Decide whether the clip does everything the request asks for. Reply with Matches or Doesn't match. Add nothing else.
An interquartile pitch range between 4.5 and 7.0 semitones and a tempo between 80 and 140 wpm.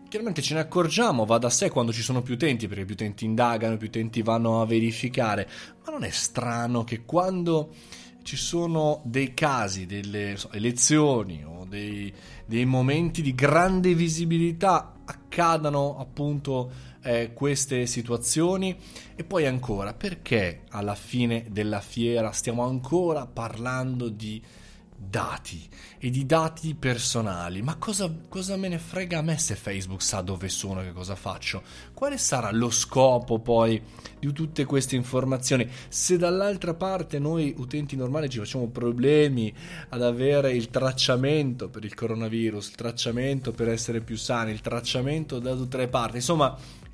Doesn't match